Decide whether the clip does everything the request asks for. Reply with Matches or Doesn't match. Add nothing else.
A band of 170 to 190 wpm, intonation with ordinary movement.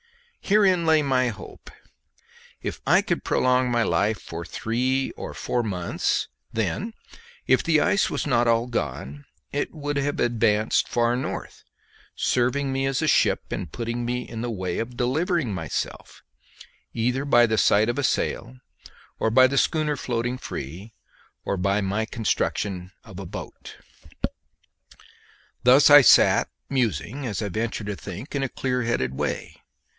Doesn't match